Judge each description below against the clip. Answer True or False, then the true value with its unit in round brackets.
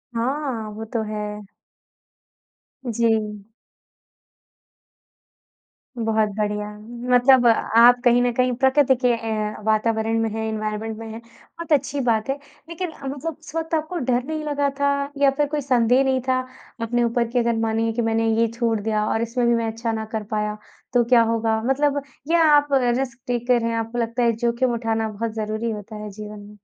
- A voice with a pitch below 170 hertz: False (235 Hz)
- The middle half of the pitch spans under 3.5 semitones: True (2.8 semitones)